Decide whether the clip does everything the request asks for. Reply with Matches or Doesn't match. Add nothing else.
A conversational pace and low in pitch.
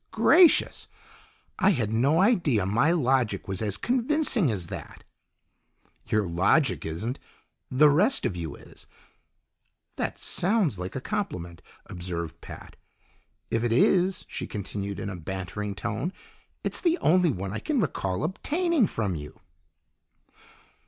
Doesn't match